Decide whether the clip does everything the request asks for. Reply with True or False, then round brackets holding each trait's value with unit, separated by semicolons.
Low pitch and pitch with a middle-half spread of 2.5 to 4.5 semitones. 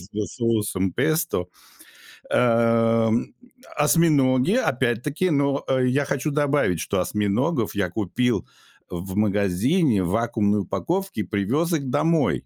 False (120 Hz; 5.9 semitones)